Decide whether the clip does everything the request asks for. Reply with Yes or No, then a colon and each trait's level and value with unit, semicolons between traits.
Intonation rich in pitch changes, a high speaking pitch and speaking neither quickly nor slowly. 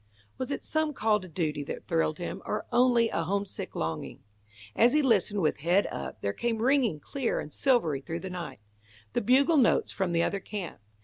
Yes: wide, 6.7 semitones; high, 200 Hz; average, 195 wpm